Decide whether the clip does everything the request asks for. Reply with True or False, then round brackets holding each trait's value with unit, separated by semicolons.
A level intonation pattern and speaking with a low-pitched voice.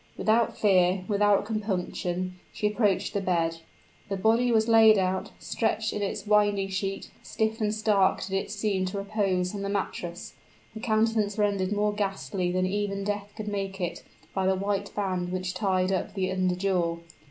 False (2.1 semitones; 200 Hz)